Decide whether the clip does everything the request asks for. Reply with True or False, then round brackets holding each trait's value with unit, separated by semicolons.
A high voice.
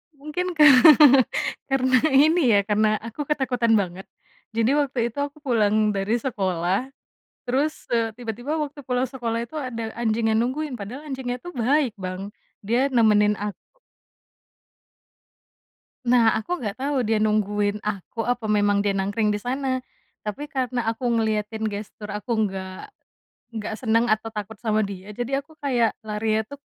True (230 Hz)